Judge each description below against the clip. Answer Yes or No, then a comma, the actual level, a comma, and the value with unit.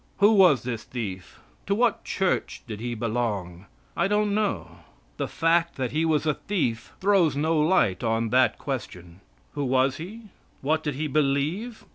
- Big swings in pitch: Yes, wide, 7.6 semitones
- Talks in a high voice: No, medium, 145 Hz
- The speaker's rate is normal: Yes, average, 165 wpm